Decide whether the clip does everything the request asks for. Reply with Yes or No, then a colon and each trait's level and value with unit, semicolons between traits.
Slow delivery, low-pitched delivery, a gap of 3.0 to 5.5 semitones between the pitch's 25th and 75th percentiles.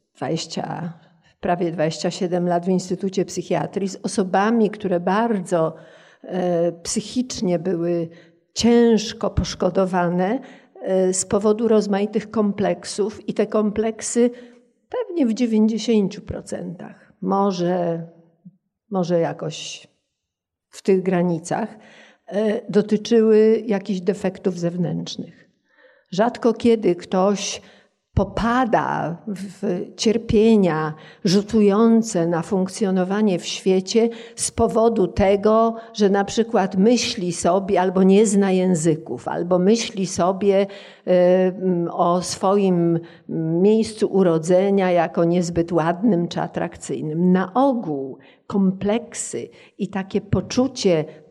No: slow, 90 wpm; high, 195 Hz; average, 3.6 semitones